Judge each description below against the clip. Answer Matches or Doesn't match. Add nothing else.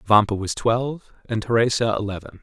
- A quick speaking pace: Doesn't match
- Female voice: Doesn't match